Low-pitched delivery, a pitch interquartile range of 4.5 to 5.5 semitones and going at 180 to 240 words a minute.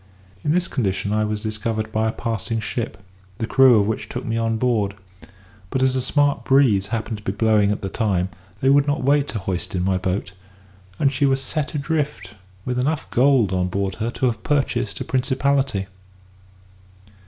Yes: low, 115 Hz; average, 4.8 semitones; average, 190 wpm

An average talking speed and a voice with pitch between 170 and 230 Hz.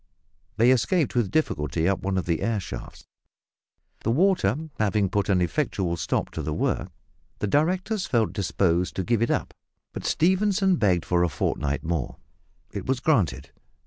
No: average, 165 wpm; low, 105 Hz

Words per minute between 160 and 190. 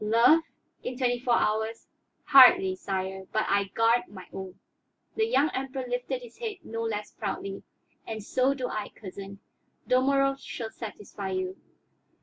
No: average, 145 wpm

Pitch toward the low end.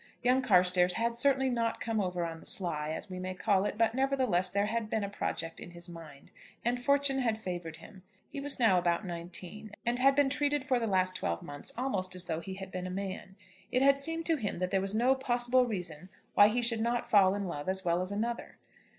No: high, 205 Hz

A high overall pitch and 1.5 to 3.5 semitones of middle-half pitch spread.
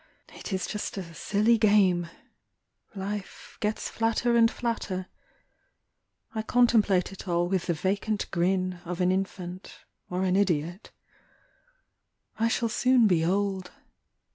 Yes: high, 195 Hz; average, 3.1 semitones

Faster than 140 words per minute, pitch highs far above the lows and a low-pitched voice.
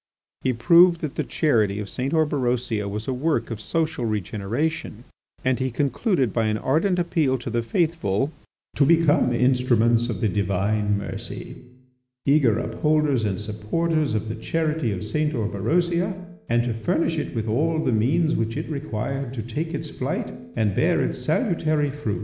Yes: average, 165 wpm; wide, 6.0 semitones; low, 125 Hz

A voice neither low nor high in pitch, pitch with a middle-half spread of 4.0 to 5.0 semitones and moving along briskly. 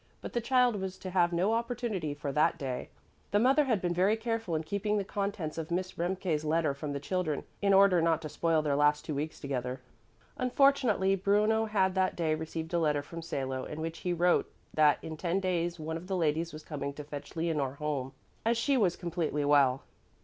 Yes: medium, 170 Hz; average, 4.6 semitones; fast, 210 wpm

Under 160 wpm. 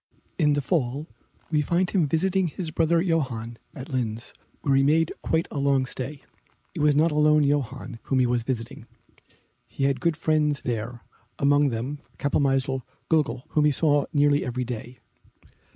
No: average, 165 wpm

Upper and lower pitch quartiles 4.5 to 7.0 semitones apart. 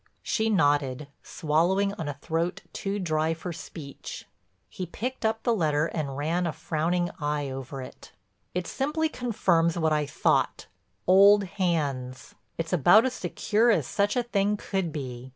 Yes: average, 5.2 semitones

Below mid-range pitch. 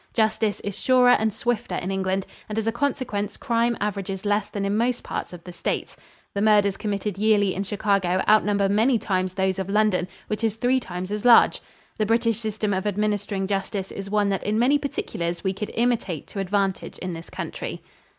No: high, 205 Hz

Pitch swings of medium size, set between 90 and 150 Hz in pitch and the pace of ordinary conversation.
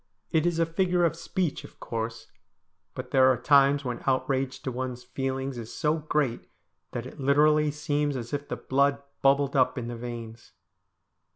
Yes: average, 3.1 semitones; low, 135 Hz; average, 175 wpm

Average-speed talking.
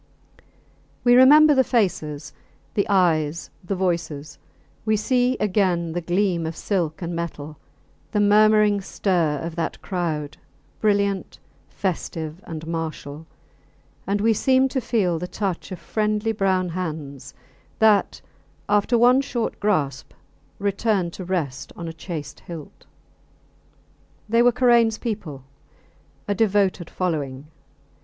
No: slow, 120 wpm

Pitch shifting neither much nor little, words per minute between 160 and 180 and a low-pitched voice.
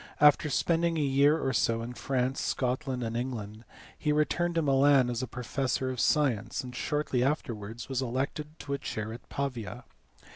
Yes: average, 3.4 semitones; average, 170 wpm; low, 130 Hz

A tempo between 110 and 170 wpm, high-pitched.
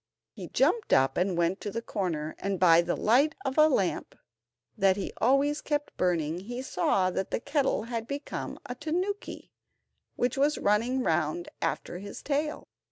Yes: average, 165 wpm; high, 220 Hz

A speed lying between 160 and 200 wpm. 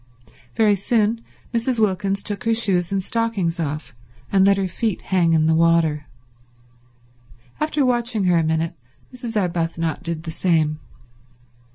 No: average, 145 wpm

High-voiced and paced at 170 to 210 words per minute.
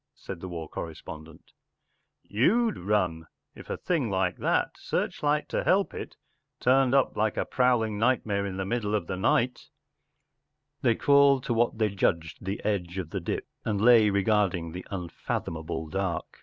No: low, 105 Hz; average, 180 wpm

